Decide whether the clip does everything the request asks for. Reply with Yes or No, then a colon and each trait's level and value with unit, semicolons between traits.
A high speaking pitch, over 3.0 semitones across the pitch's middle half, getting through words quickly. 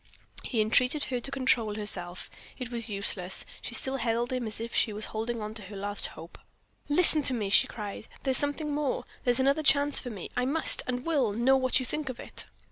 Yes: high, 245 Hz; average, 4.0 semitones; fast, 210 wpm